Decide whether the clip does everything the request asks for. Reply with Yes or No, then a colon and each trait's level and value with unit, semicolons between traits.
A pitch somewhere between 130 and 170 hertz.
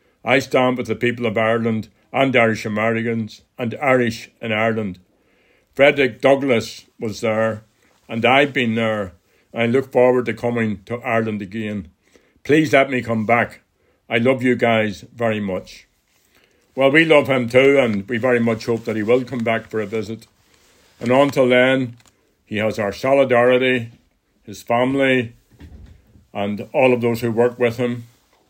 No: low, 115 Hz